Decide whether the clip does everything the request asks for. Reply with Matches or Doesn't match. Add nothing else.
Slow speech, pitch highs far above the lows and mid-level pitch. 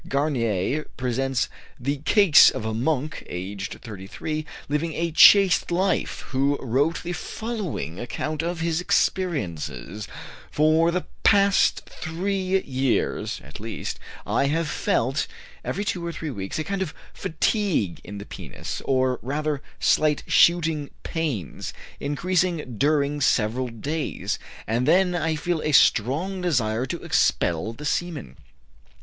Matches